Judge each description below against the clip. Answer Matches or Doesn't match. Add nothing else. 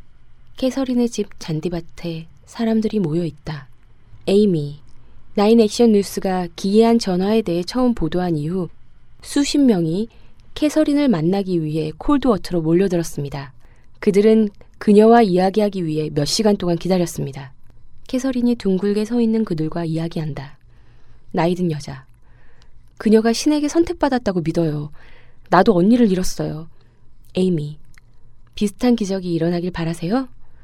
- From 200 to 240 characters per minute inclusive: Doesn't match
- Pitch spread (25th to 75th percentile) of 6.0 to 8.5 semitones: Matches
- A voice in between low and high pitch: Matches